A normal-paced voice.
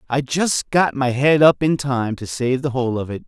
No: fast, 255 wpm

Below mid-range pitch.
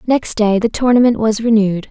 No: high, 220 Hz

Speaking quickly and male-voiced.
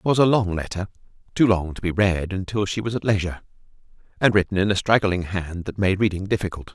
Yes: fast, 225 wpm; male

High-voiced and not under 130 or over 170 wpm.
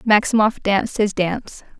Yes: high, 210 Hz; slow, 135 wpm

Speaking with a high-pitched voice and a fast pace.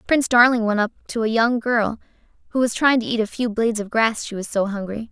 Yes: high, 225 Hz; fast, 260 wpm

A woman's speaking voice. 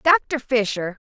Yes: female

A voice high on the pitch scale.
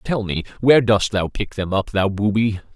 No: low, 105 Hz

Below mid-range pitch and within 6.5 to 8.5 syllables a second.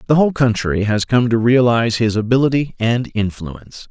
No: low, 120 Hz; 5.4 syllables/s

